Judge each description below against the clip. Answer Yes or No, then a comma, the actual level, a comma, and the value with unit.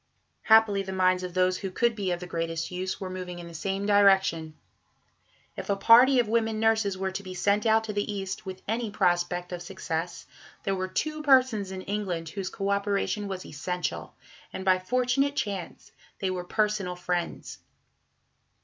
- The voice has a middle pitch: No, high, 195 Hz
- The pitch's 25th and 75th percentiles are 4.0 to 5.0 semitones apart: No, average, 2.7 semitones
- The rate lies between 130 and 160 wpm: No, average, 180 wpm